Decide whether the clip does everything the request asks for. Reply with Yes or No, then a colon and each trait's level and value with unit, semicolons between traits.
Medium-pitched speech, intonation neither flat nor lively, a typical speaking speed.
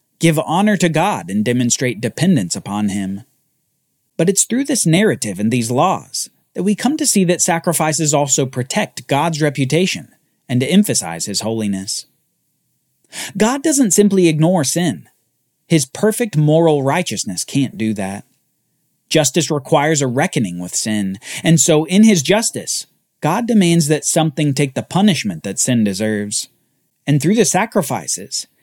No: medium, 155 Hz; wide, 6.8 semitones; average, 145 wpm